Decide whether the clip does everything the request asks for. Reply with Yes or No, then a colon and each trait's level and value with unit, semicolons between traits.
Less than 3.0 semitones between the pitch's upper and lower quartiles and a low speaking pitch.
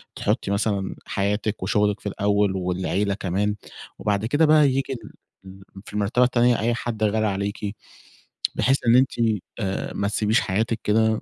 Yes: narrow, 2.4 semitones; low, 105 Hz